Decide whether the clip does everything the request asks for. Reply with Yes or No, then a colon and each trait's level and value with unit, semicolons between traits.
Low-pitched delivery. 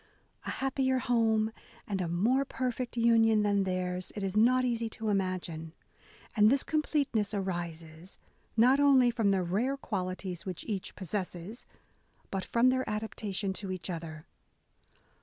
No: high, 210 Hz